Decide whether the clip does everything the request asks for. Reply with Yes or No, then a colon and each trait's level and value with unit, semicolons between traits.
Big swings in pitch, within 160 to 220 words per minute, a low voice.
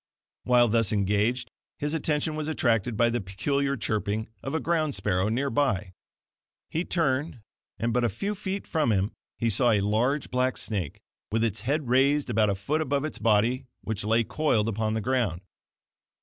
No: average, 4.9 semitones; average, 180 wpm; low, 120 Hz